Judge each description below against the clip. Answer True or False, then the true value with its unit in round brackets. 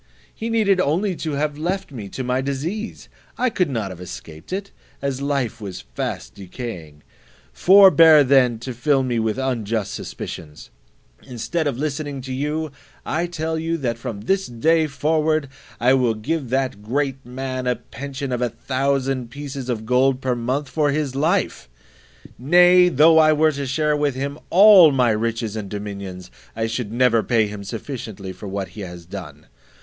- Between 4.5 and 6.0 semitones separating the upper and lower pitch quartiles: True (5.1 semitones)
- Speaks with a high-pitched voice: False (130 Hz)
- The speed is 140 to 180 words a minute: True (170 wpm)